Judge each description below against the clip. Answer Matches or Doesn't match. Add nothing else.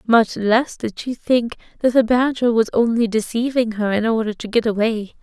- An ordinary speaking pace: Matches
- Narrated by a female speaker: Matches